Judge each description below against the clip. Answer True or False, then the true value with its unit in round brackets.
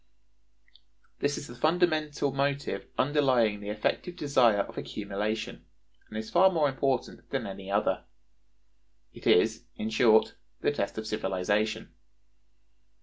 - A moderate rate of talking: False (125 wpm)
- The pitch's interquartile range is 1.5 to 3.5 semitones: False (5.2 semitones)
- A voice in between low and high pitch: False (120 Hz)